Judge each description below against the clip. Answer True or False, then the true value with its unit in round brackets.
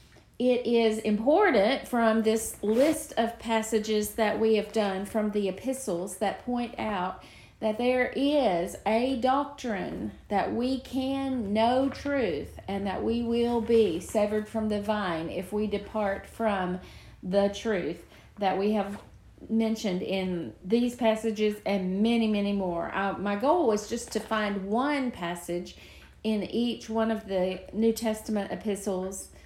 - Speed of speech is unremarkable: True (145 wpm)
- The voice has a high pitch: True (220 Hz)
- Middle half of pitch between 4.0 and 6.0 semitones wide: False (2.8 semitones)